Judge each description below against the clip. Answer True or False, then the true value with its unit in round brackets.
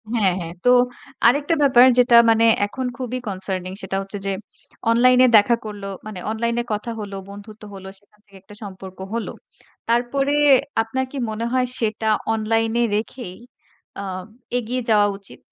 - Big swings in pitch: False (3.5 semitones)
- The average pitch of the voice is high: True (220 Hz)